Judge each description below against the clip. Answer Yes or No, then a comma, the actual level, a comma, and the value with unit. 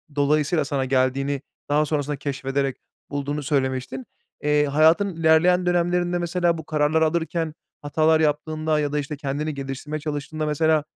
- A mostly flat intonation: Yes, narrow, 2.1 semitones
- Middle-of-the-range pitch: Yes, medium, 150 Hz